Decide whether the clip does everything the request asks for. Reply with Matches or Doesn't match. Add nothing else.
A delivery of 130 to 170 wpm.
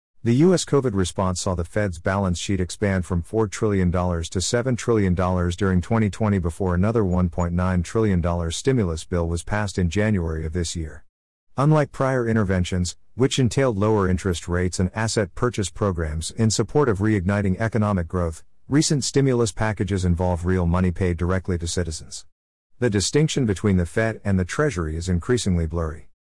Matches